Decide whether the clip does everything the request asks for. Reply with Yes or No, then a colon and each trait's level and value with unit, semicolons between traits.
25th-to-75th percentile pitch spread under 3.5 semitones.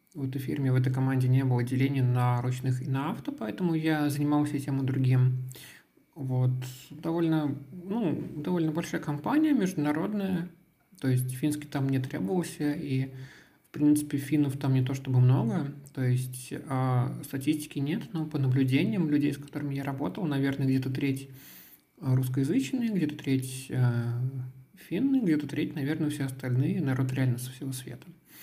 Yes: average, 2.8 semitones